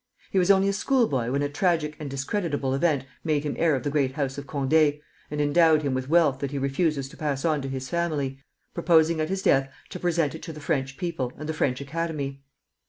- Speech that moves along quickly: Yes, fast, 235 wpm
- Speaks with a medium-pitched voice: Yes, medium, 150 Hz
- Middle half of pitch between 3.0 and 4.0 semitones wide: Yes, average, 3.4 semitones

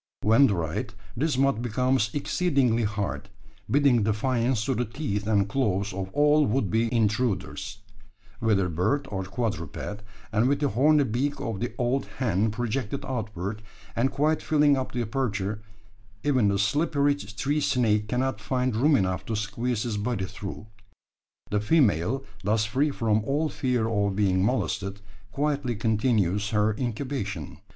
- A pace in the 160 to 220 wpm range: No, average, 145 wpm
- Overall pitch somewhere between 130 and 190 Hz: No, low, 115 Hz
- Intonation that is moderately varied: Yes, average, 4.6 semitones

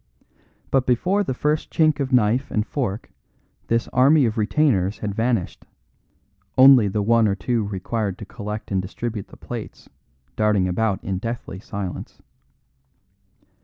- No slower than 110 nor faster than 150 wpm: Yes, average, 140 wpm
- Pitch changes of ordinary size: Yes, average, 4.0 semitones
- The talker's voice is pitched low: Yes, low, 110 Hz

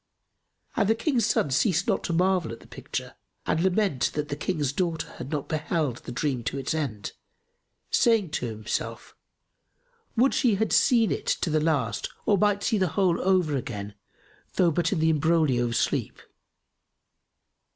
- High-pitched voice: No, medium, 160 Hz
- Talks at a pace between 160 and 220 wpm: Yes, average, 170 wpm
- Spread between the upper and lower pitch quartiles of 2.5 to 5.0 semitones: No, wide, 5.5 semitones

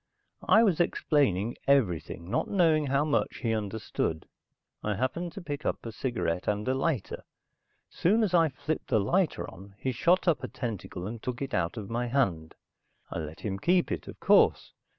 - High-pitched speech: No, low, 125 Hz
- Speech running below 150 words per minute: No, average, 185 wpm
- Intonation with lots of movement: Yes, wide, 7.6 semitones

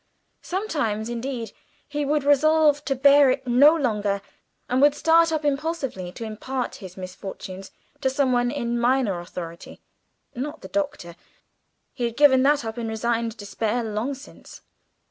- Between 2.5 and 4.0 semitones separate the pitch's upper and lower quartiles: No, average, 4.6 semitones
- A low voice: No, very high, 255 Hz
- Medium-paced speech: Yes, average, 150 wpm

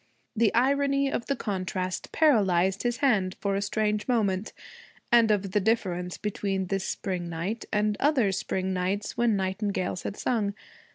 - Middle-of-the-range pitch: No, high, 205 Hz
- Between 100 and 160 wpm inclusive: Yes, average, 155 wpm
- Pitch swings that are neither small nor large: Yes, average, 3.5 semitones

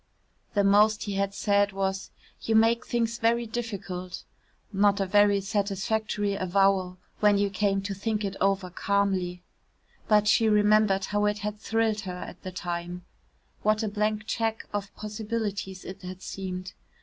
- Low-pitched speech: No, high, 205 Hz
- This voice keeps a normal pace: Yes, average, 155 wpm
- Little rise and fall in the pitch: Yes, narrow, 1.8 semitones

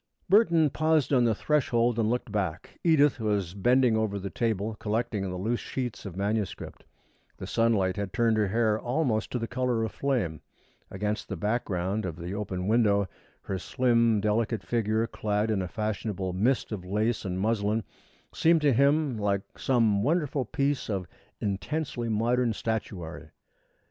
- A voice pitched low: Yes, low, 110 Hz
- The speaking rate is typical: Yes, average, 160 wpm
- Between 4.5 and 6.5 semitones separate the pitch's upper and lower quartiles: No, average, 3.5 semitones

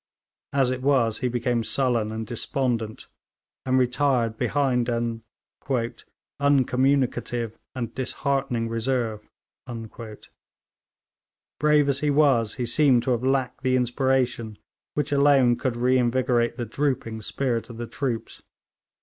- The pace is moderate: No, slow, 115 wpm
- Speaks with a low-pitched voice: Yes, low, 125 Hz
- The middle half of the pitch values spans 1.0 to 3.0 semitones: Yes, narrow, 2.5 semitones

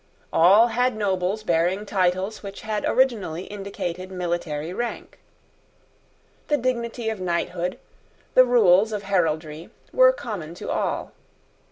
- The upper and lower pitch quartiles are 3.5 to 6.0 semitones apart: Yes, average, 4.0 semitones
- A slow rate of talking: Yes, slow, 120 wpm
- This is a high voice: Yes, high, 195 Hz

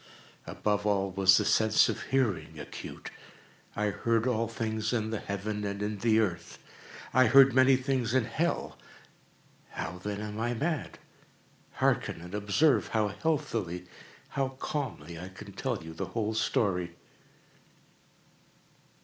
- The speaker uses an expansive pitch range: No, average, 4.1 semitones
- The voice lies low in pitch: Yes, low, 110 Hz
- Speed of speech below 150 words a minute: Yes, slow, 135 wpm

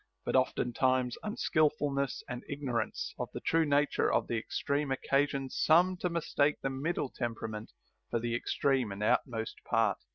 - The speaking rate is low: No, average, 155 wpm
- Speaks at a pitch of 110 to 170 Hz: Yes, low, 135 Hz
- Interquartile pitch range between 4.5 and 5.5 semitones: No, average, 3.7 semitones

